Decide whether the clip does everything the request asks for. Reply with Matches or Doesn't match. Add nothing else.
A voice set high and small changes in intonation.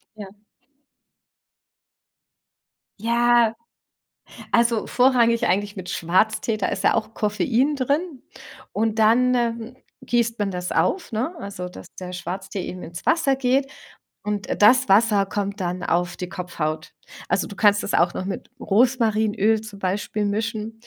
Doesn't match